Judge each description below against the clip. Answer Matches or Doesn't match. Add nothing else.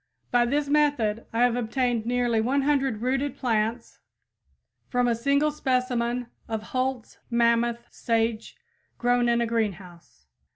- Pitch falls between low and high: Doesn't match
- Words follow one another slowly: Matches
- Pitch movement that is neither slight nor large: Doesn't match